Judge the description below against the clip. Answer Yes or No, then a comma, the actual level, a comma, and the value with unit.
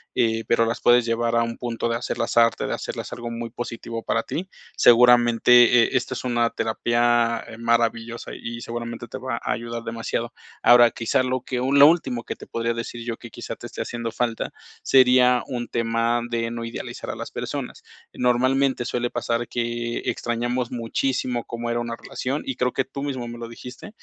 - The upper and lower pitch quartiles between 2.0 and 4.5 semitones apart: No, narrow, 1.0 semitones